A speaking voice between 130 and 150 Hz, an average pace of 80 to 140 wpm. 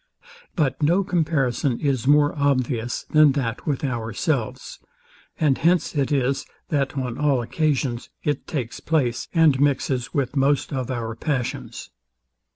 Yes: low, 135 Hz; slow, 135 wpm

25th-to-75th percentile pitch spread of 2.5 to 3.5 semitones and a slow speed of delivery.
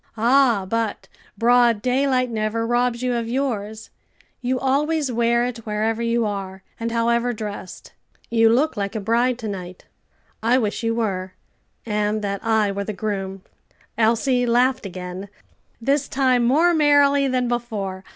No: average, 3.1 semitones; average, 150 wpm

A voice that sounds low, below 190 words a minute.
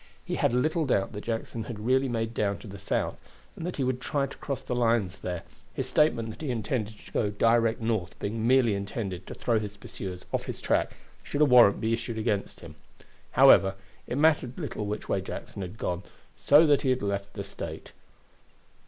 No: low, 115 Hz; fast, 205 wpm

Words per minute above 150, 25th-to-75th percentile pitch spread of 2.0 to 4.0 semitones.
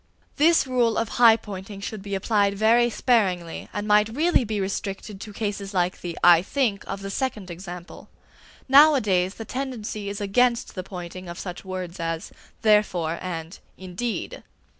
Yes: average, 160 wpm; average, 3.7 semitones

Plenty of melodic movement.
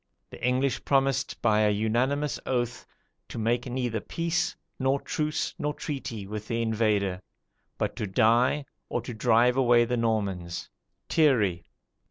No: average, 3.8 semitones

